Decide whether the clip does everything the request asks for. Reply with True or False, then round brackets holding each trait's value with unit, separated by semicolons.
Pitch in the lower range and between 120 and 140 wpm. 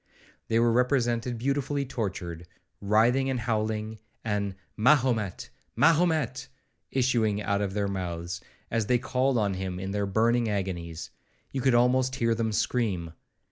True (115 Hz; 135 wpm)